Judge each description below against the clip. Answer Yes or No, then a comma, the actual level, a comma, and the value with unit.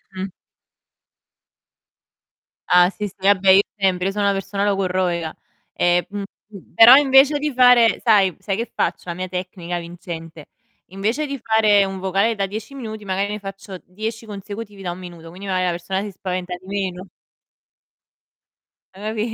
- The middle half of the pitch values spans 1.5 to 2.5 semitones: No, average, 2.9 semitones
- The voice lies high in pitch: Yes, high, 195 Hz